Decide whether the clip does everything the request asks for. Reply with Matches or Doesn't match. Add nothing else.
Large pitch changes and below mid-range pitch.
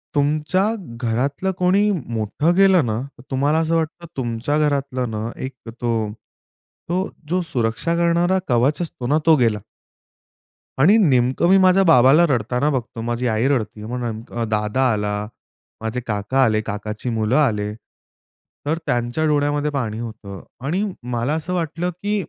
Matches